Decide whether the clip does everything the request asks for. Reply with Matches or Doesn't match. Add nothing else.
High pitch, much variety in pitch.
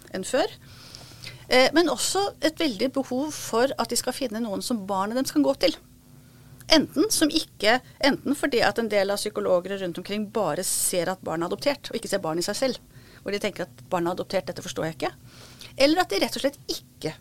Matches